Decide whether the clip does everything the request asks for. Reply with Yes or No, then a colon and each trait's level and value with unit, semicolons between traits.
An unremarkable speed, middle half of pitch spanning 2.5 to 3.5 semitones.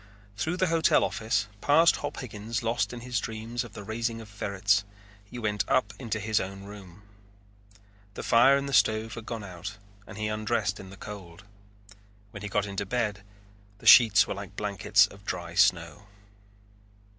Yes: average, 180 wpm; average, 2.8 semitones